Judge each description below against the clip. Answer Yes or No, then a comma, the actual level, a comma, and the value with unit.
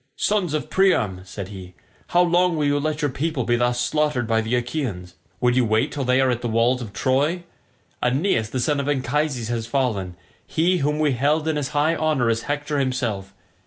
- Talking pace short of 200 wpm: No, fast, 205 wpm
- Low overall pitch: Yes, low, 130 Hz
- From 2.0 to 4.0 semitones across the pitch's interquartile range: No, average, 4.6 semitones